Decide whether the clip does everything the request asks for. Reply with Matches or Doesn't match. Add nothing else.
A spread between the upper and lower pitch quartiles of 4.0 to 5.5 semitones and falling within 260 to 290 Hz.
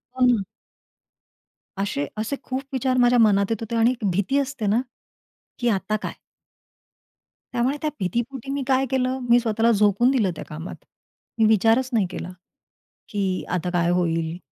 Doesn't match